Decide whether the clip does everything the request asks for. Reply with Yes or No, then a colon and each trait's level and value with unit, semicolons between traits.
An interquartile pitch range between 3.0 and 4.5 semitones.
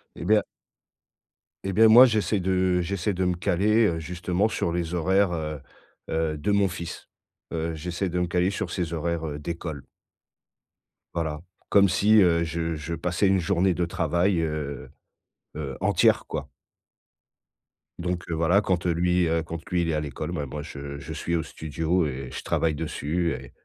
No: narrow, 2.4 semitones